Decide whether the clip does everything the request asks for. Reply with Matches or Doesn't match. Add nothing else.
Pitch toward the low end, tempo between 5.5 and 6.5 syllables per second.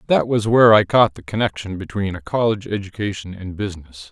Matches